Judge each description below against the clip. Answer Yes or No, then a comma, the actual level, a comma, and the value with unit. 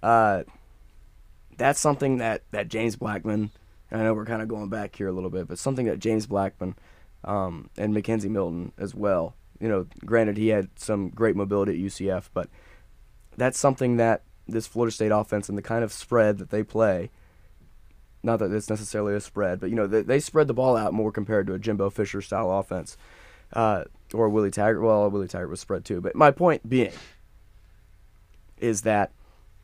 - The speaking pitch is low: Yes, low, 105 Hz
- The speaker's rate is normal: Yes, average, 190 wpm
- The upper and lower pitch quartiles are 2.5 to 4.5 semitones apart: Yes, average, 3.2 semitones